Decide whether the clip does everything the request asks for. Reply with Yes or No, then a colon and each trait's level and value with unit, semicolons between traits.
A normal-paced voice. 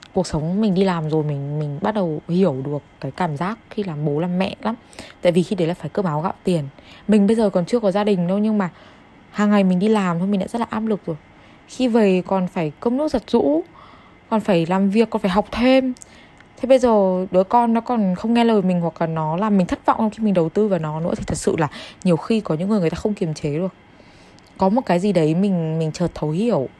No: fast, 270 wpm